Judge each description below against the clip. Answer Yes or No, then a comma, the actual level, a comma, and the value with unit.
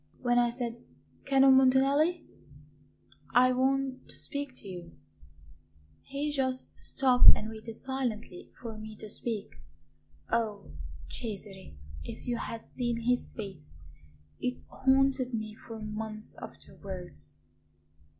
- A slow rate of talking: Yes, slow, 115 wpm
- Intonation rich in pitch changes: No, average, 3.6 semitones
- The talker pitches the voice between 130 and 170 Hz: No, high, 240 Hz